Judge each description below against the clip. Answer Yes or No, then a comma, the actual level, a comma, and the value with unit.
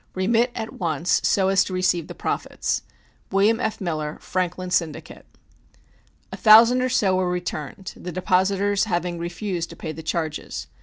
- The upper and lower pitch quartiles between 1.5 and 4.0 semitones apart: Yes, average, 3.0 semitones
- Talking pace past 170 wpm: No, average, 155 wpm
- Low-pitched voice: No, medium, 185 Hz